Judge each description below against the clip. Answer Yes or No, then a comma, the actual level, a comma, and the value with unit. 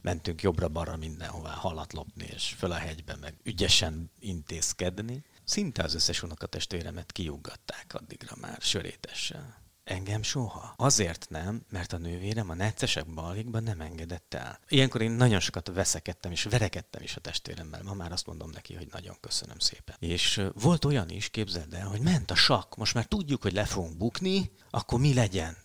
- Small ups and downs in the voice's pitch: No, average, 5.0 semitones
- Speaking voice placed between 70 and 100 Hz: Yes, very low, 95 Hz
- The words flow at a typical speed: No, fast, 165 wpm